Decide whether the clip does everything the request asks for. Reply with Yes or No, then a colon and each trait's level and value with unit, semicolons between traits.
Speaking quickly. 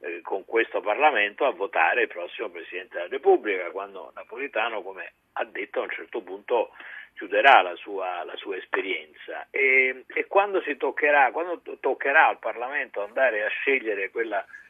No: average, 160 wpm